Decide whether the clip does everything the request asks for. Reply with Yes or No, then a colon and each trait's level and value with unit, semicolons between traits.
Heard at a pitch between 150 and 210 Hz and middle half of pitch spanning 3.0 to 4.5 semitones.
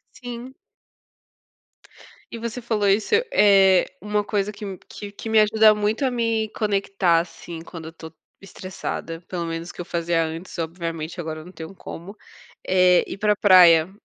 Yes: high, 190 Hz; average, 4.0 semitones